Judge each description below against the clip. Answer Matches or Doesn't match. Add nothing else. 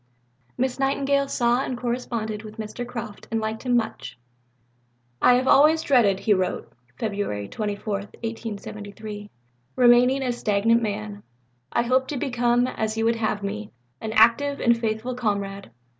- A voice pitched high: Matches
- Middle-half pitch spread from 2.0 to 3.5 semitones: Matches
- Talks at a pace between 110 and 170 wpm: Matches